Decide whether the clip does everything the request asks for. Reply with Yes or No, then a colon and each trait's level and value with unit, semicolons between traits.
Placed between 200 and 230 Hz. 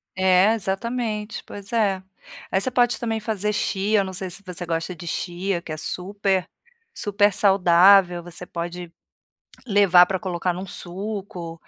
No: high, 190 Hz